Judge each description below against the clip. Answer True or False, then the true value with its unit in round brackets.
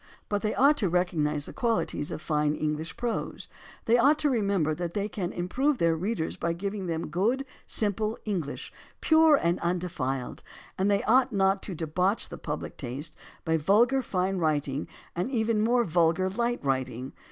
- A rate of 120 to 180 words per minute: True (175 wpm)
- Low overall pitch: False (185 Hz)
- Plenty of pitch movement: True (5.8 semitones)